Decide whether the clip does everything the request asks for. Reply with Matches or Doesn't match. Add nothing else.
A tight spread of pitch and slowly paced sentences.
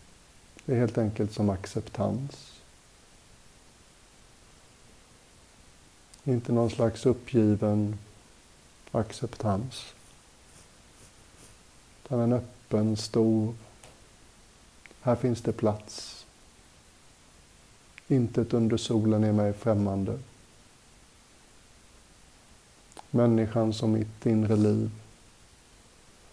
Matches